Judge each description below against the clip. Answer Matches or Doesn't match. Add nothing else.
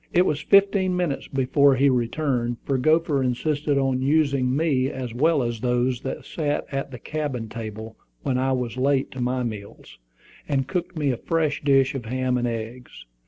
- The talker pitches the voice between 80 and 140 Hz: Matches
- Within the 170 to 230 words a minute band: Matches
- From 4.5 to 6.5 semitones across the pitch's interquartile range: Doesn't match